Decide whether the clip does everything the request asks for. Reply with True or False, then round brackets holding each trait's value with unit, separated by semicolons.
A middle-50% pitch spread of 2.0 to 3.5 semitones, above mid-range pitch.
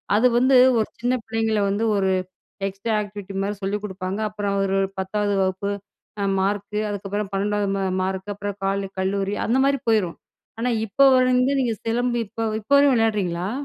True (2.5 semitones; 205 Hz)